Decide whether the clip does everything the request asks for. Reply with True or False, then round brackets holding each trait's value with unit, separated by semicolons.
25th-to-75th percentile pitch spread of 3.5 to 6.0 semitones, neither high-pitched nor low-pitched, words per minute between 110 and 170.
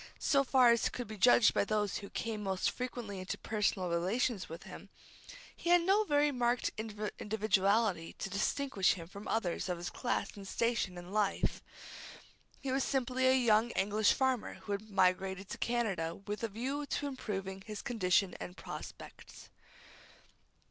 False (4.2 semitones; 215 Hz; 160 wpm)